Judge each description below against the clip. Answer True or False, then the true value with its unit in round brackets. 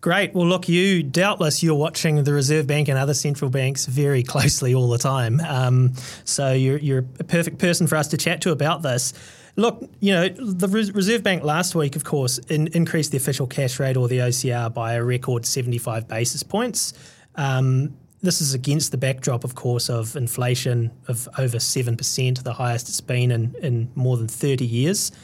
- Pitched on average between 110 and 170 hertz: True (135 Hz)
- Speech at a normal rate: True (195 wpm)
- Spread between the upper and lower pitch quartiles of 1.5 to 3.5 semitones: False (4.0 semitones)